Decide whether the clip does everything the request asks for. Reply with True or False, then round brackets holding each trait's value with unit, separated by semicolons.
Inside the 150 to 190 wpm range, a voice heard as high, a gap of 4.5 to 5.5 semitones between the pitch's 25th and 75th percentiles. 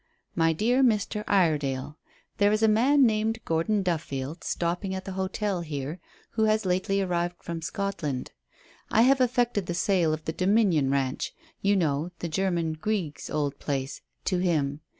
False (160 wpm; 180 Hz; 5.2 semitones)